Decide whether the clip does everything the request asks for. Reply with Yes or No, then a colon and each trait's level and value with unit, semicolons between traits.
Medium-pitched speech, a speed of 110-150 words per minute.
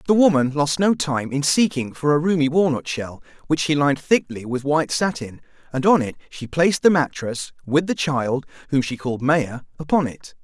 No: medium, 145 Hz; average, 200 wpm